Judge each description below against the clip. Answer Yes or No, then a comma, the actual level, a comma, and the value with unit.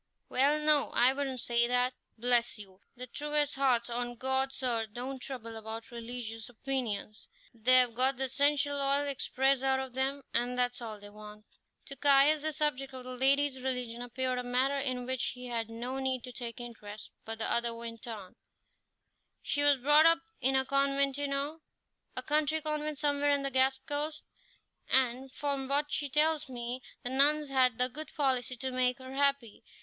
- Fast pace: No, average, 185 wpm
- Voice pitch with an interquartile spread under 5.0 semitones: Yes, narrow, 2.5 semitones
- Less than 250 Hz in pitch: No, very high, 260 Hz